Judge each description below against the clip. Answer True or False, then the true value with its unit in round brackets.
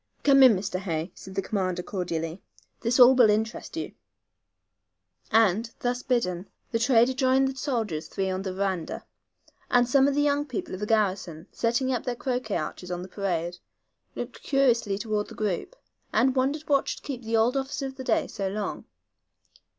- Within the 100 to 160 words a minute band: False (180 wpm)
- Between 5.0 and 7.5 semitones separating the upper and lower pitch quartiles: True (5.5 semitones)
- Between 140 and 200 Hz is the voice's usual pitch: False (225 Hz)